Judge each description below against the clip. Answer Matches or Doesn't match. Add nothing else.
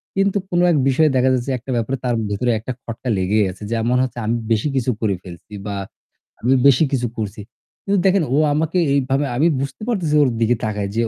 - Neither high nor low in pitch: Doesn't match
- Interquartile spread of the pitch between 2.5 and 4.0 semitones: Doesn't match